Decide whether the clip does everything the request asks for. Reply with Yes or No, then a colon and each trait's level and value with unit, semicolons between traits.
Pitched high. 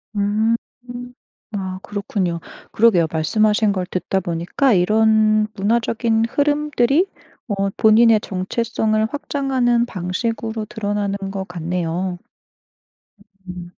Yes: high, 215 Hz